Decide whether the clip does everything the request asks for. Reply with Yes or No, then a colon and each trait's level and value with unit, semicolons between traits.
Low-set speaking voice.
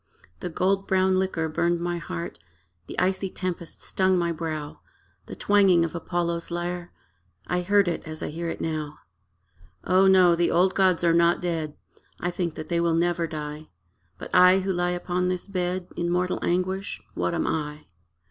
No: medium, 175 Hz